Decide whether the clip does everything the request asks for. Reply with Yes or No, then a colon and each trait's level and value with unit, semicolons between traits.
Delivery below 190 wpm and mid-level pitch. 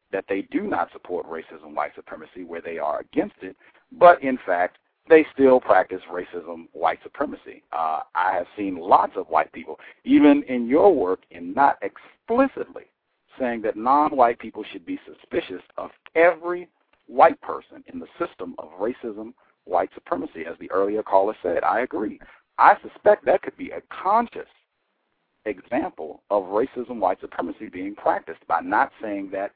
Yes: average, 165 wpm; medium, 175 Hz